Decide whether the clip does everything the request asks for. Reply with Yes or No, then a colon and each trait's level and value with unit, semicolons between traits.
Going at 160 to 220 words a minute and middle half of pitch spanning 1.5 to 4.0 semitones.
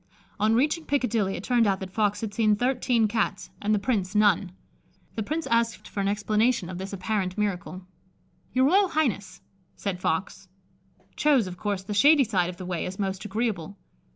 Yes: average, 180 wpm; average, 3.6 semitones